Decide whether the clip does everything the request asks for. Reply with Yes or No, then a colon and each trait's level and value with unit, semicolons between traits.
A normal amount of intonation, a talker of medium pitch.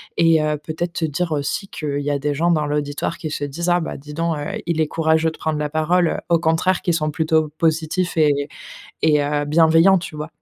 No: narrow, 2.0 semitones; medium, 160 Hz